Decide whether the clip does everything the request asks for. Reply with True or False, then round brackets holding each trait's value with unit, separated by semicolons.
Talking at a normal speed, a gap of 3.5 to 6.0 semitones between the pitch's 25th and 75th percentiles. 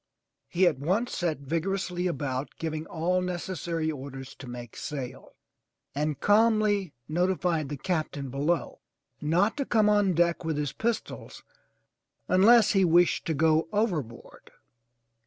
False (130 wpm; 4.4 semitones)